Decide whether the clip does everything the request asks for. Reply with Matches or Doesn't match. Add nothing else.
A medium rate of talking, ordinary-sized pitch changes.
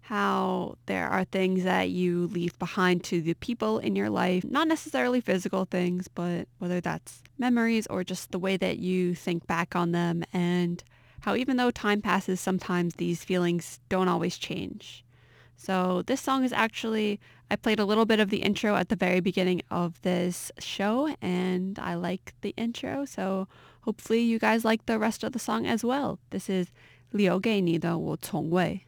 Matches